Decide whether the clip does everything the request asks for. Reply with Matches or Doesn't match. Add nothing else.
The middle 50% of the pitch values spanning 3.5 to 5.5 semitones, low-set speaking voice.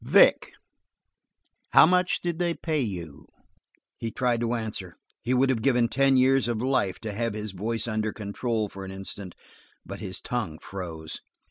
Matches